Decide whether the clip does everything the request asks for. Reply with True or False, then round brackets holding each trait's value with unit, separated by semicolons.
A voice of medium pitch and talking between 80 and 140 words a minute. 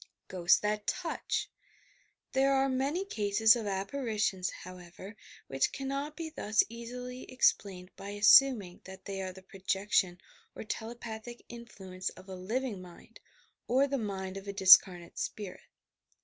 False (210 Hz; 135 wpm)